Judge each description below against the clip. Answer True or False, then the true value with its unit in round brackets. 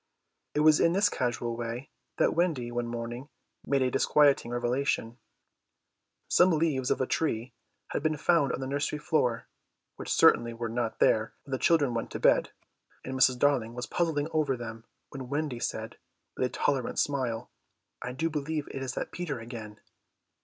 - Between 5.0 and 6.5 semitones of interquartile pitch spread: False (3.8 semitones)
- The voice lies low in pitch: True (130 Hz)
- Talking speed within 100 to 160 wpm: False (175 wpm)